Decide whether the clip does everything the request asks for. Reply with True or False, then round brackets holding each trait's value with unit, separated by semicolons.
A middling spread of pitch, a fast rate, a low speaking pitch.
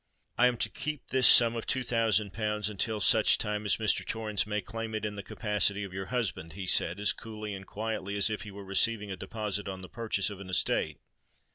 False (2.2 semitones; 230 wpm; 105 Hz)